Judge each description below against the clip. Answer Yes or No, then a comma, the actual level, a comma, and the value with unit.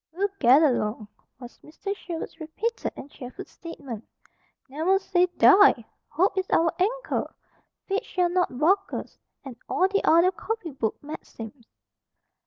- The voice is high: Yes, very high, 335 Hz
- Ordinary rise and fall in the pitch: No, wide, 6.3 semitones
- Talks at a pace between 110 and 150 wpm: Yes, average, 140 wpm